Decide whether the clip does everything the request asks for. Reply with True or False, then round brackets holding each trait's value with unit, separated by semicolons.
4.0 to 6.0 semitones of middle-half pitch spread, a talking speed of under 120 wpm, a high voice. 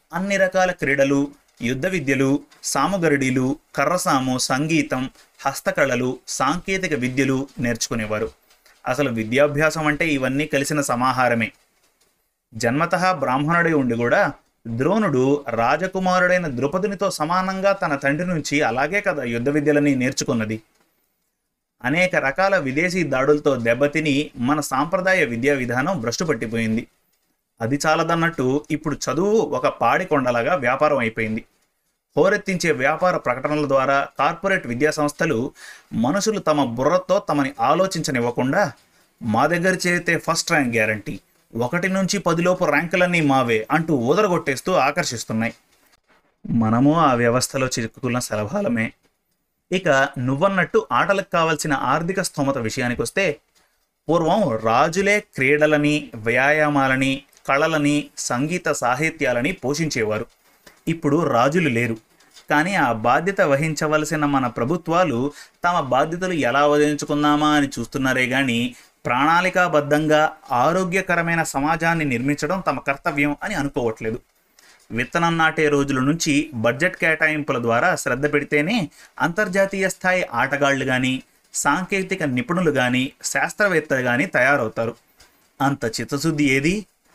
False (4.6 semitones; 100 wpm; 145 Hz)